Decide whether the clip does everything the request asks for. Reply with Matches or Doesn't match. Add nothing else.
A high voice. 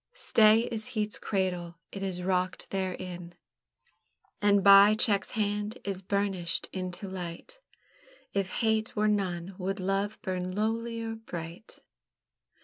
Matches